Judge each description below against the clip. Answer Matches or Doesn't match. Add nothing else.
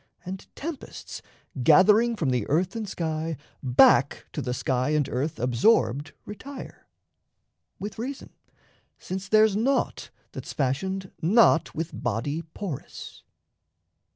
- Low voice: Doesn't match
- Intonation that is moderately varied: Doesn't match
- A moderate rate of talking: Doesn't match